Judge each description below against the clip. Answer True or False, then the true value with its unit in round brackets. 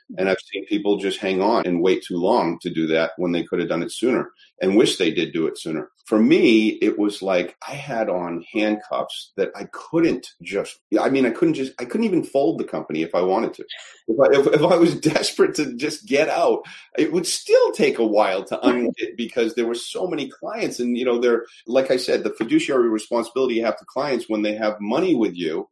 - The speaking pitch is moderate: False (120 Hz)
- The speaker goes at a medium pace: False (235 wpm)